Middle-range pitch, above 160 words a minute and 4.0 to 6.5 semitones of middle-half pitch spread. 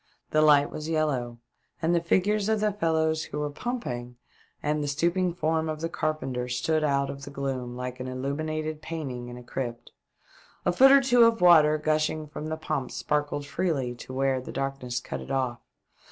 No: medium, 150 Hz; average, 190 wpm; average, 3.6 semitones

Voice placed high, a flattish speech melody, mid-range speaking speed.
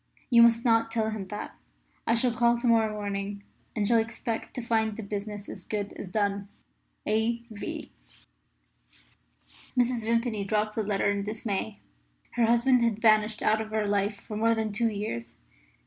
Yes: high, 220 Hz; narrow, 2.0 semitones; average, 170 wpm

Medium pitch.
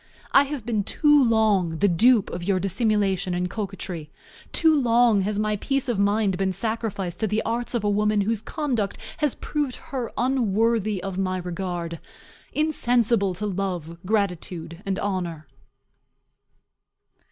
No: high, 205 Hz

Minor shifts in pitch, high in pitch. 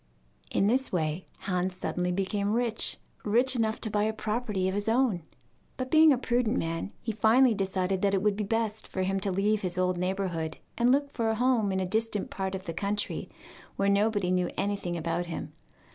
No: average, 3.2 semitones; high, 205 Hz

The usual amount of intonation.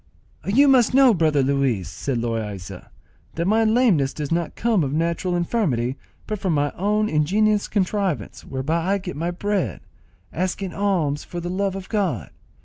No: wide, 6.2 semitones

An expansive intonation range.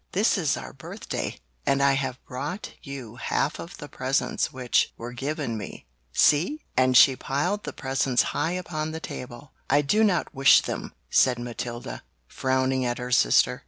No: average, 3.1 semitones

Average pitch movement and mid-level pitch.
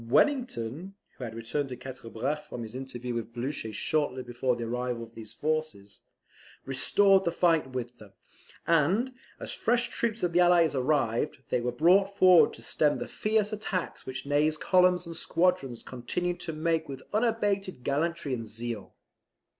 No: wide, 6.6 semitones; medium, 145 Hz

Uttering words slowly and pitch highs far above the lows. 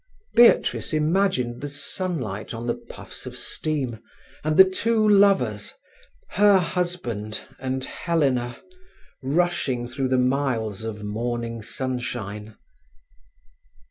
Yes: slow, 105 wpm; wide, 6.8 semitones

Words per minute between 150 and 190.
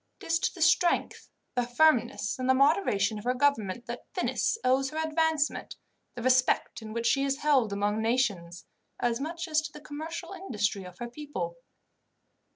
Yes: average, 175 wpm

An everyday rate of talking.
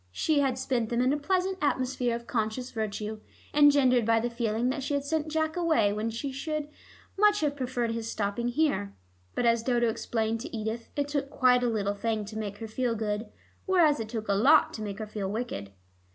No: fast, 210 wpm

